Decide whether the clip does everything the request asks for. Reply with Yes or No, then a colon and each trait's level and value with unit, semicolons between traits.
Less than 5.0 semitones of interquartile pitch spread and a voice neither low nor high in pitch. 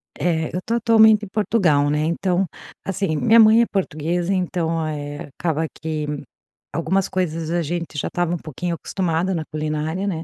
Yes: average, 3.4 semitones; medium, 170 Hz